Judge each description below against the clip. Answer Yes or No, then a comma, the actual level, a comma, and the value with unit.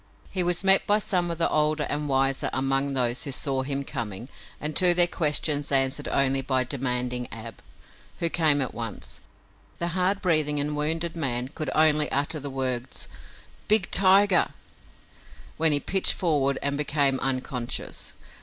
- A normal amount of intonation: Yes, average, 3.8 semitones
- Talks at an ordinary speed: Yes, average, 160 wpm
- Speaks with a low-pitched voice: No, medium, 145 Hz